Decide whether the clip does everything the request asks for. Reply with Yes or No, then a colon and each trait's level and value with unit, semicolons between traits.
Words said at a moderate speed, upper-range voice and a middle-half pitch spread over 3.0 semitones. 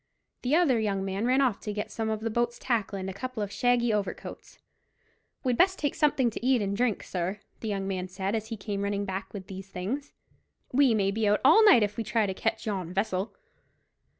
No: fast, 225 wpm; high, 215 Hz; average, 3.8 semitones